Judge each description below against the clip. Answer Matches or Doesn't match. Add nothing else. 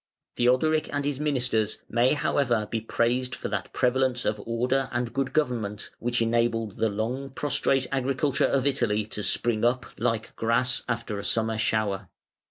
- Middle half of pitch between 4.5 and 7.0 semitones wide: Doesn't match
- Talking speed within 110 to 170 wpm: Matches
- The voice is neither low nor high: Doesn't match